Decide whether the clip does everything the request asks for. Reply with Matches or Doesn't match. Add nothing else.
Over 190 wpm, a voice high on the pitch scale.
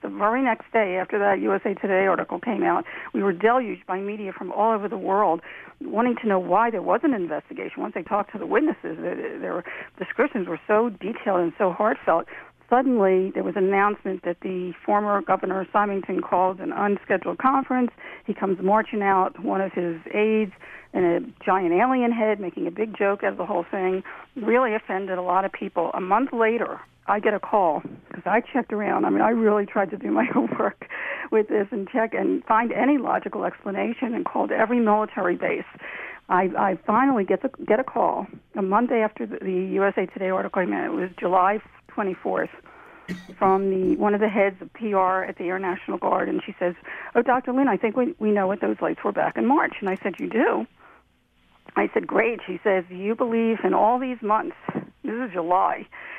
Matches